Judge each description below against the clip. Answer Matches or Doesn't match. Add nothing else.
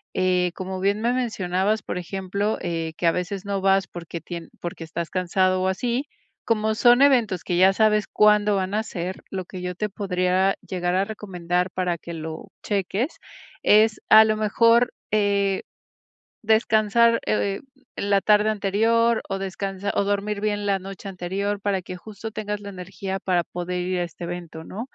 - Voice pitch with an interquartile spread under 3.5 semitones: Matches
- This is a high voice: Matches